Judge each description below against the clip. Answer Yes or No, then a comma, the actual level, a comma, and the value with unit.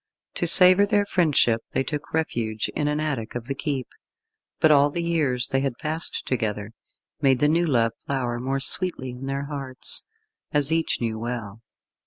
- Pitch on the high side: No, low, 135 Hz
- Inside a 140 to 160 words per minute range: No, average, 175 wpm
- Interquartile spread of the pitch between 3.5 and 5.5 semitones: Yes, average, 4.3 semitones